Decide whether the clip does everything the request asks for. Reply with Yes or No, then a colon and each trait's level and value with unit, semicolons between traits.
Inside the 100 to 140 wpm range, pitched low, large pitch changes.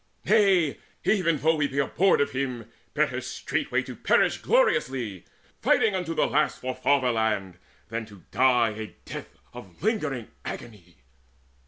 Yes: slow, 135 wpm; low, 130 Hz; wide, 6.5 semitones